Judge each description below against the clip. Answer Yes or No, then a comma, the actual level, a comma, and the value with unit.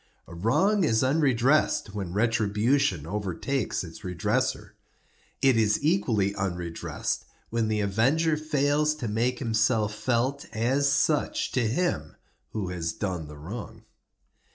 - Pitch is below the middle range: Yes, low, 115 Hz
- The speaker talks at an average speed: No, slow, 125 wpm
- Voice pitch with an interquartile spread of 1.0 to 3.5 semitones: No, wide, 5.6 semitones